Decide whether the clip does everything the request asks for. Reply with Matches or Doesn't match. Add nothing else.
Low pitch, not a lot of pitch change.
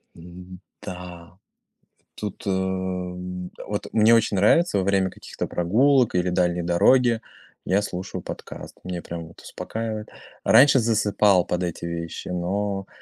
Doesn't match